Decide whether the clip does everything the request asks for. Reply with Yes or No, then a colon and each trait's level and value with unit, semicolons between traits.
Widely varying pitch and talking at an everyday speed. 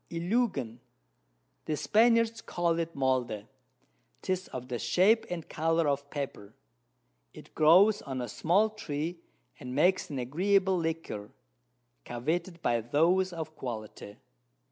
No: wide, 6.2 semitones; slow, 120 wpm